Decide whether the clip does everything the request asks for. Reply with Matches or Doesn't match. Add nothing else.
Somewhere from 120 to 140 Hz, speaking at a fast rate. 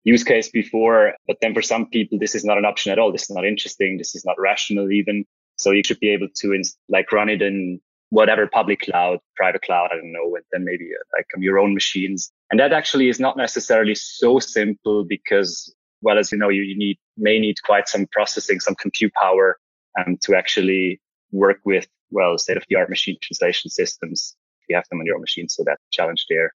Doesn't match